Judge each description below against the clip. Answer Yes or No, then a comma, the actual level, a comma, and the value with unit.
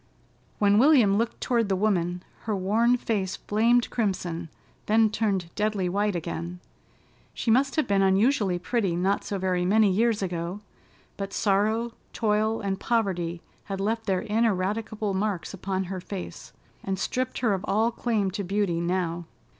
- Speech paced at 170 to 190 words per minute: No, average, 155 wpm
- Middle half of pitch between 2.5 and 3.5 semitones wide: Yes, average, 3.1 semitones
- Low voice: No, high, 200 Hz